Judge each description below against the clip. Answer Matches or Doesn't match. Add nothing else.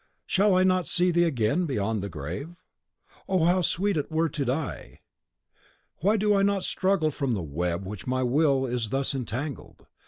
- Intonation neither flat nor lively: Doesn't match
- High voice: Doesn't match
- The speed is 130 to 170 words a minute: Doesn't match